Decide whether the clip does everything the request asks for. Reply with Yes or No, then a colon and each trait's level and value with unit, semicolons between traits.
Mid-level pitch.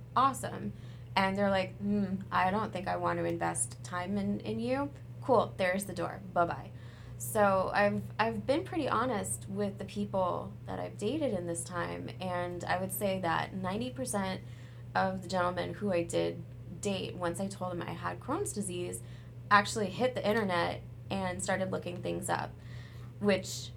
No: low, 125 Hz